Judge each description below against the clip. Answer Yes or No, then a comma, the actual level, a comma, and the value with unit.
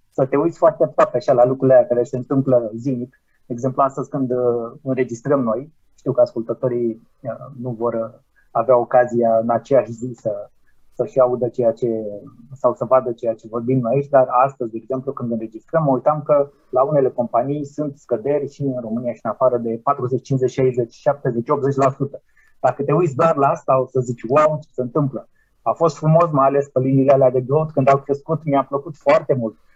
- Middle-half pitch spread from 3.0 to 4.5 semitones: No, narrow, 2.6 semitones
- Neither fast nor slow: No, fast, 200 wpm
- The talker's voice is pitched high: No, low, 130 Hz